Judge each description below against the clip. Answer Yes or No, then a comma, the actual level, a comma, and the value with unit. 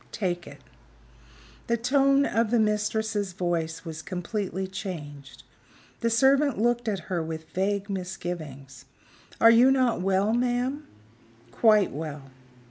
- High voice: Yes, high, 200 Hz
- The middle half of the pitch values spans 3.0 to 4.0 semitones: No, wide, 5.5 semitones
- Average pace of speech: No, slow, 125 wpm